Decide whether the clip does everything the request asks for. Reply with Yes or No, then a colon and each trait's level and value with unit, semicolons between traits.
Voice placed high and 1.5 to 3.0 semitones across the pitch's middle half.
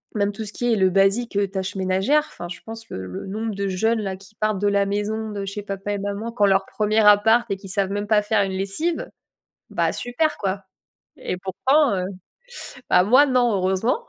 Yes: high, 205 Hz; narrow, 2.4 semitones